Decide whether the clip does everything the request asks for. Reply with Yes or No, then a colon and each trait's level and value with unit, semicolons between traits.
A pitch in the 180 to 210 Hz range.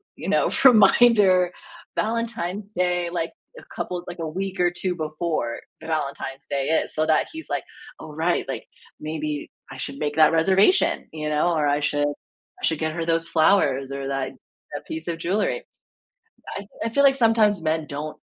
No: medium, 165 Hz